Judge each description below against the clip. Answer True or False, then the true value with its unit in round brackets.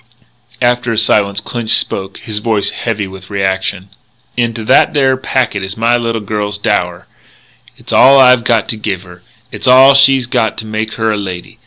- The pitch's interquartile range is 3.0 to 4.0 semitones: True (3.3 semitones)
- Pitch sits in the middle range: False (110 Hz)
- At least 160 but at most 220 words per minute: True (180 wpm)